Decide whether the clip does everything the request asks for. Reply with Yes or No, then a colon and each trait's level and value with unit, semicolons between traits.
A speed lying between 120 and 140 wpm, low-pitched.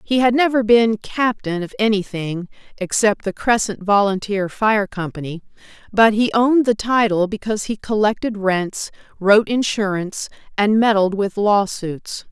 No: slow, 135 wpm; high, 210 Hz